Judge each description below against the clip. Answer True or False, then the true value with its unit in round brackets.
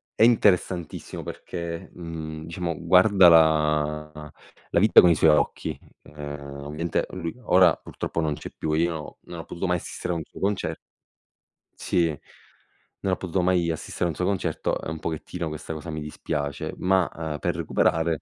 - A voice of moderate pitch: False (80 Hz)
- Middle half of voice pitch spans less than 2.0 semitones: False (2.6 semitones)